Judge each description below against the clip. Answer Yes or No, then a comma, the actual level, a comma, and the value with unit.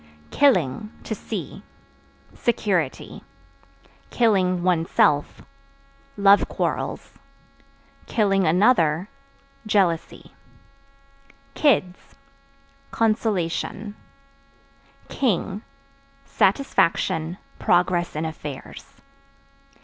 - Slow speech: Yes, slow, 50 wpm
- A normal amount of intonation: Yes, average, 4.2 semitones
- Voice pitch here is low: No, medium, 185 Hz